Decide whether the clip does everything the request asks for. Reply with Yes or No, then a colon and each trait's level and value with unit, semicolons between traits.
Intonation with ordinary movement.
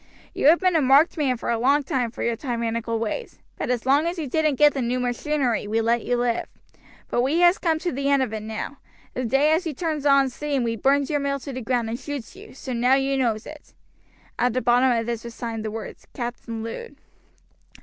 Yes: average, 3.8 semitones